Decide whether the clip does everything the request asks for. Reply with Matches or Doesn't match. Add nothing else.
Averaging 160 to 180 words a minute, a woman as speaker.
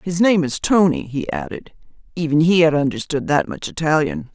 Matches